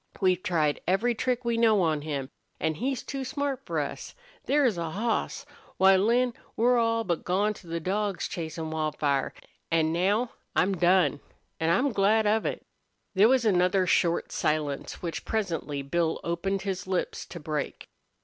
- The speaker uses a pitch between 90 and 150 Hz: No, high, 190 Hz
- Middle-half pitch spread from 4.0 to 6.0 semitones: Yes, wide, 5.5 semitones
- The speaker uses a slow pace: No, average, 165 wpm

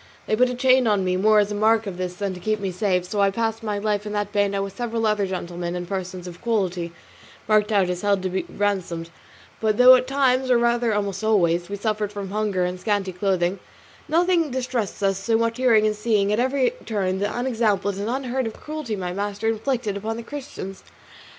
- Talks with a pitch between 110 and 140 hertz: No, high, 210 Hz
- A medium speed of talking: No, fast, 220 wpm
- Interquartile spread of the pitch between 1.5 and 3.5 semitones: Yes, average, 3.2 semitones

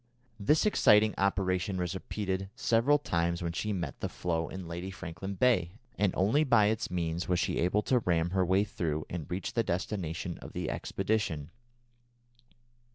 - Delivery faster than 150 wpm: Yes, average, 165 wpm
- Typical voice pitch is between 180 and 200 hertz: No, very low, 95 Hz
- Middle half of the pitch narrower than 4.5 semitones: Yes, average, 3.5 semitones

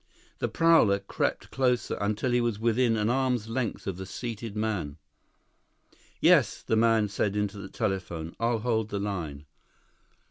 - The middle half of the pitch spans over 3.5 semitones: No, average, 3.1 semitones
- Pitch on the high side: No, low, 110 Hz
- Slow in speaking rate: No, average, 150 wpm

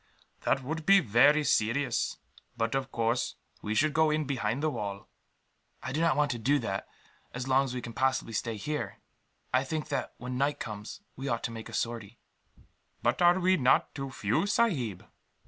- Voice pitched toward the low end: Yes, low, 130 Hz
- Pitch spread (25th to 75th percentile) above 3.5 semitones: Yes, average, 4.5 semitones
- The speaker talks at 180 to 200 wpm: Yes, average, 190 wpm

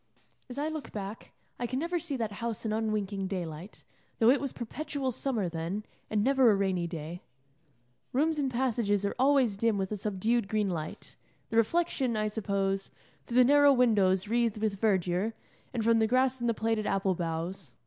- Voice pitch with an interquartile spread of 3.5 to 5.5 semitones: Yes, average, 4.3 semitones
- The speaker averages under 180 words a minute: No, average, 185 wpm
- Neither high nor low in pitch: No, high, 220 Hz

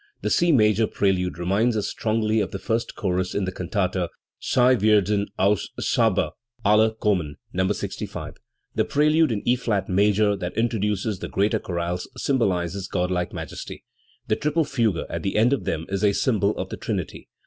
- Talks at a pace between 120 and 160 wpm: No, average, 175 wpm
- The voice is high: No, low, 105 Hz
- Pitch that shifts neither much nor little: Yes, average, 3.2 semitones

